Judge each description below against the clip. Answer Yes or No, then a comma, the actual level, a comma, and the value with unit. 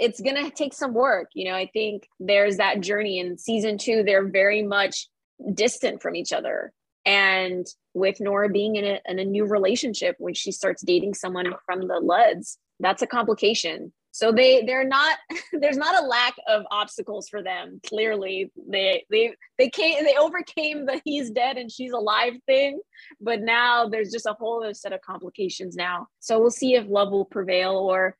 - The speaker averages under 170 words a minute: No, average, 185 wpm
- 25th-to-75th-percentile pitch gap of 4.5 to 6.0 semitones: Yes, average, 4.9 semitones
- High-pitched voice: Yes, high, 210 Hz